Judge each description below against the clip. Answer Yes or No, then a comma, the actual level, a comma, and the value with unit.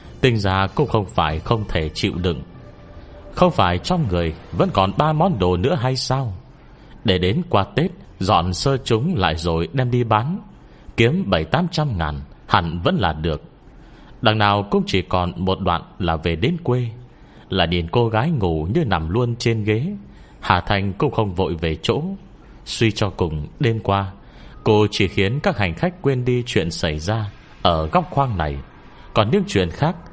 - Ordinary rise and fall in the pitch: No, wide, 6.3 semitones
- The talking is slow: No, average, 185 wpm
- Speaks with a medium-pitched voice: No, low, 105 Hz